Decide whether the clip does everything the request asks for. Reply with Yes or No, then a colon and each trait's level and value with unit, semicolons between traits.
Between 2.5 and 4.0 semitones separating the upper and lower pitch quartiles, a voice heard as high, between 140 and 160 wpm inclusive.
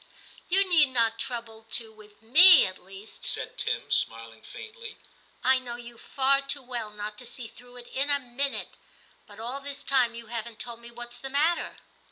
No: average, 3.6 semitones; high, 240 Hz; average, 200 wpm